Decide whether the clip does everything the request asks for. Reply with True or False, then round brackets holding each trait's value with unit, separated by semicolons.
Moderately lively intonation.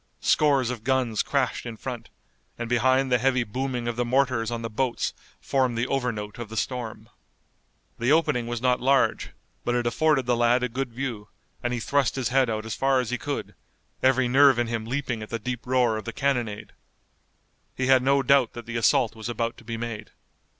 False (2.3 semitones)